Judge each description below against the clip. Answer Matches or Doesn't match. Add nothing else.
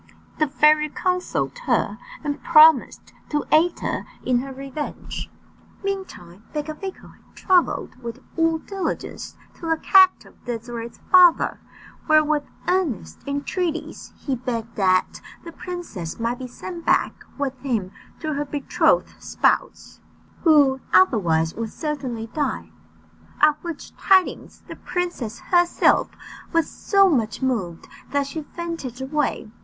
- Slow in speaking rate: Matches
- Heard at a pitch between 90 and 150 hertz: Doesn't match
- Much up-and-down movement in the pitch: Matches